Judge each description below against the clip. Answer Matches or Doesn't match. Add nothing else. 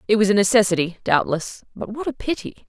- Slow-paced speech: Doesn't match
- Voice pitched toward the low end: Doesn't match